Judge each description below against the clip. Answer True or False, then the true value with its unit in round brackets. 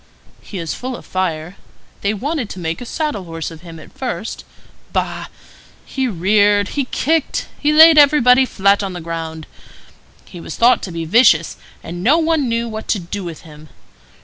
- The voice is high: True (205 Hz)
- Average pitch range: False (7.3 semitones)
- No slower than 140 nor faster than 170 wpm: False (180 wpm)